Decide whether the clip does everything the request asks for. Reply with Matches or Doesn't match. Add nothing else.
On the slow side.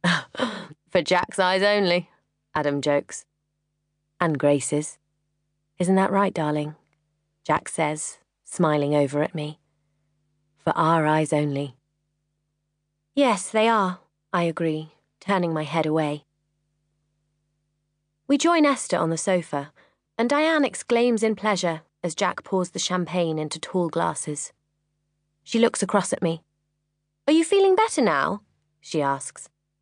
Matches